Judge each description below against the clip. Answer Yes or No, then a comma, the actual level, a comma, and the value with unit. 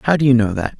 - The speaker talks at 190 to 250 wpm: No, fast, 375 wpm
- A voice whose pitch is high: No, low, 125 Hz